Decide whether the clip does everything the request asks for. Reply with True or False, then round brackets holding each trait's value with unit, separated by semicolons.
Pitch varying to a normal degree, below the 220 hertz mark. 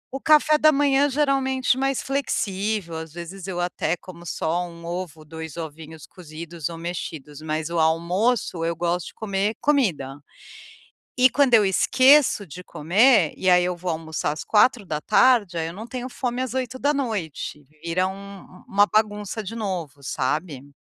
False (6.7 semitones; 185 Hz)